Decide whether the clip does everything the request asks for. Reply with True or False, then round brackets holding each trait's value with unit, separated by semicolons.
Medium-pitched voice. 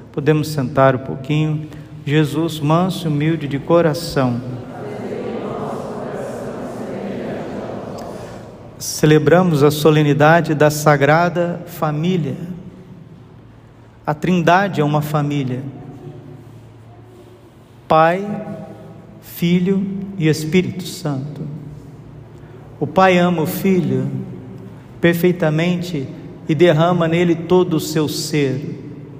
True (155 Hz)